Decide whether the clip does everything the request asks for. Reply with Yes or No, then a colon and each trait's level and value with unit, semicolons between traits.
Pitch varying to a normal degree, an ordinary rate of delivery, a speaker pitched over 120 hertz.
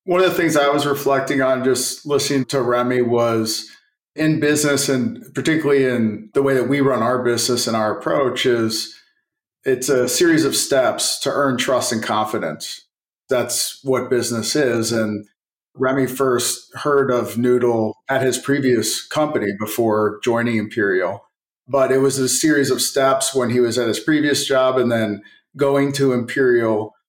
Yes: average, 3.0 semitones; average, 165 wpm; low, 130 Hz